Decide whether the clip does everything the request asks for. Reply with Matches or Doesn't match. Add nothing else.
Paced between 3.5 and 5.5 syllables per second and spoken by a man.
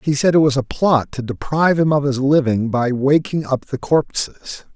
Matches